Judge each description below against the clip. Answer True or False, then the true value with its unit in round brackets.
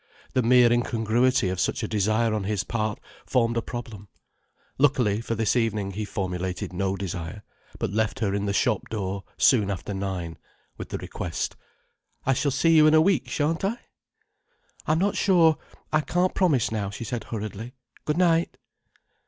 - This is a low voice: True (110 Hz)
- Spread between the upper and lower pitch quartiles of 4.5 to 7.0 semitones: True (5.2 semitones)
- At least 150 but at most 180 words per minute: True (170 wpm)